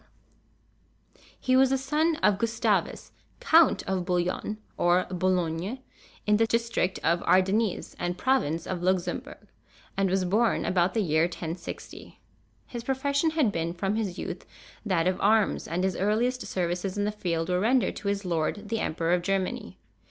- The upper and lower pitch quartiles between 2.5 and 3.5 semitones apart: No, average, 4.3 semitones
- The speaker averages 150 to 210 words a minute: Yes, average, 160 wpm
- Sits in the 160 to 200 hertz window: Yes, high, 190 Hz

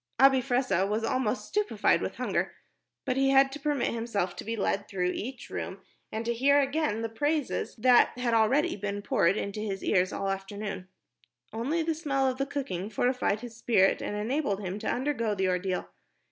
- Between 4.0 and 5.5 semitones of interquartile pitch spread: Yes, average, 4.9 semitones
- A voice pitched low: No, high, 230 Hz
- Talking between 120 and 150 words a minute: No, average, 190 wpm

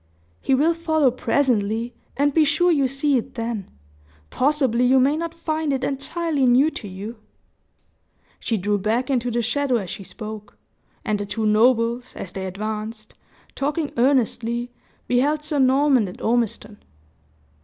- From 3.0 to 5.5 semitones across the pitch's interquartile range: Yes, average, 4.6 semitones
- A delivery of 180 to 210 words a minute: No, average, 150 wpm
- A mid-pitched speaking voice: No, very high, 250 Hz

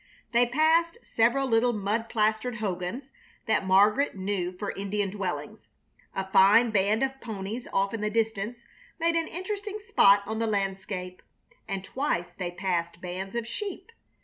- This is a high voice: Yes, high, 215 Hz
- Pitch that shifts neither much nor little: Yes, average, 4.2 semitones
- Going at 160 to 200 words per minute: No, average, 150 wpm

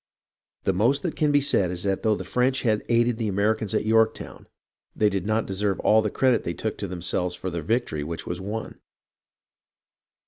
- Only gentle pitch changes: No, average, 3.6 semitones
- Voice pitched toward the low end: Yes, low, 105 Hz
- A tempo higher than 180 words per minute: Yes, average, 200 wpm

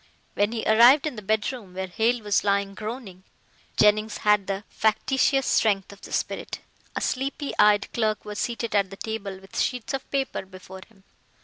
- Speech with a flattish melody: No, average, 3.0 semitones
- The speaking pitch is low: No, high, 215 Hz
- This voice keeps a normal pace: Yes, average, 180 wpm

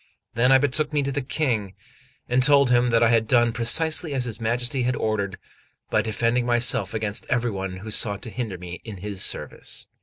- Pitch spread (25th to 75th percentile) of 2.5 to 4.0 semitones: Yes, average, 2.9 semitones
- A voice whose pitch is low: Yes, low, 120 Hz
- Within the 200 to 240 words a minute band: Yes, fast, 205 wpm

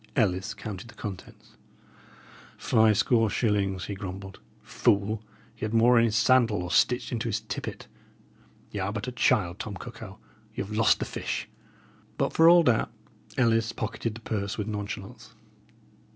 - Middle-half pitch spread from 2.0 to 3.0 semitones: Yes, narrow, 2.6 semitones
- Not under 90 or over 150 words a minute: No, average, 160 wpm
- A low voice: Yes, low, 110 Hz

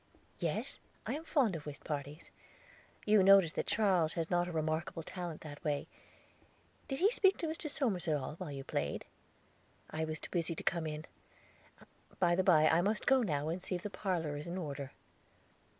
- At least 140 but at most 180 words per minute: No, average, 195 wpm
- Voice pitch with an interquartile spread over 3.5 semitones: Yes, average, 4.1 semitones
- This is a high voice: No, medium, 170 Hz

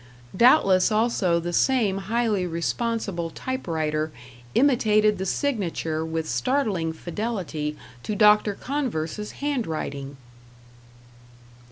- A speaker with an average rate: No, slow, 85 wpm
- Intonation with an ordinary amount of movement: No, wide, 6.1 semitones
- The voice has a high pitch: Yes, high, 195 Hz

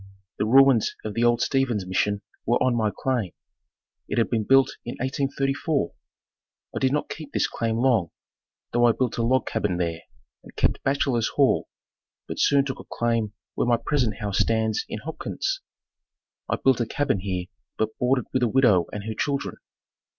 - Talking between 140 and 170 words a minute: No, average, 180 wpm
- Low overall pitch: Yes, low, 120 Hz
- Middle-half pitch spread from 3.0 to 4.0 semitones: Yes, average, 3.6 semitones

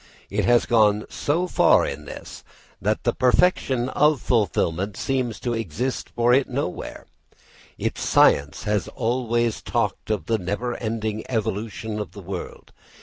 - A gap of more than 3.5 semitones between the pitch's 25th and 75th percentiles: No, average, 3.0 semitones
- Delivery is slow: No, average, 145 wpm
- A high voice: No, low, 115 Hz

